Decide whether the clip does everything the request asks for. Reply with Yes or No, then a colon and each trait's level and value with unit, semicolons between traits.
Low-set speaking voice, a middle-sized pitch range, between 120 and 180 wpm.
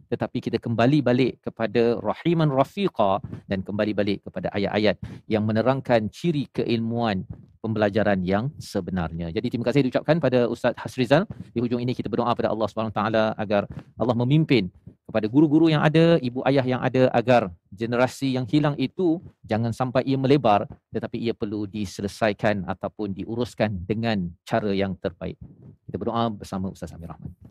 Yes: low, 115 Hz; average, 3.7 semitones; fast, 155 wpm